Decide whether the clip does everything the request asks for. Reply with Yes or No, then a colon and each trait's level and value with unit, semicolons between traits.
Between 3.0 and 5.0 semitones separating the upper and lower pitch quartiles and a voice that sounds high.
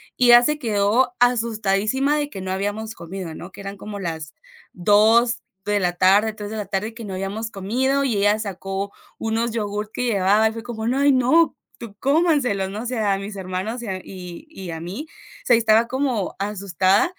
Yes: average, 3.7 semitones; high, 215 Hz